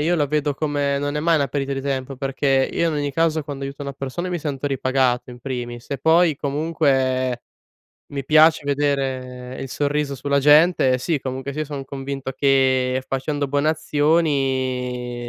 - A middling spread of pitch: No, narrow, 2.2 semitones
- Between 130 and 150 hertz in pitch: Yes, medium, 140 Hz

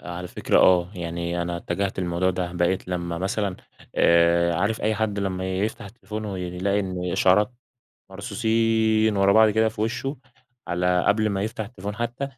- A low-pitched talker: Yes, very low, 95 Hz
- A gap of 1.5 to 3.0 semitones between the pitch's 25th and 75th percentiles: No, average, 3.4 semitones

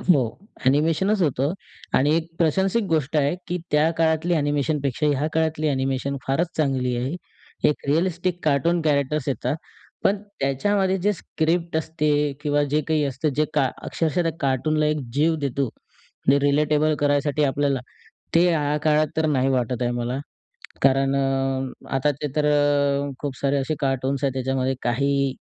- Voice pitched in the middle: Yes, medium, 145 Hz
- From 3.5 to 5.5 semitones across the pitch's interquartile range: No, narrow, 2.6 semitones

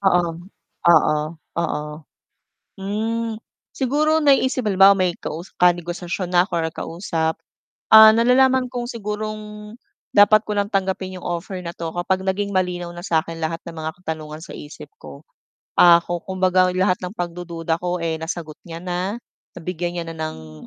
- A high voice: No, medium, 180 Hz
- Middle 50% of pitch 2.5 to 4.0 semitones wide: Yes, average, 3.6 semitones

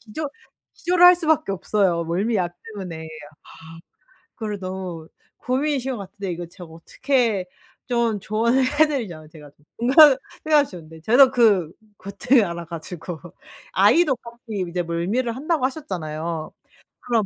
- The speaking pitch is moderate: No, high, 205 Hz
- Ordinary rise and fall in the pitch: No, wide, 7.0 semitones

